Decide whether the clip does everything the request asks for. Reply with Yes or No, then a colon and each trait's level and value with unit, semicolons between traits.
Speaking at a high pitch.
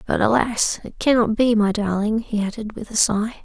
Yes: high, 220 Hz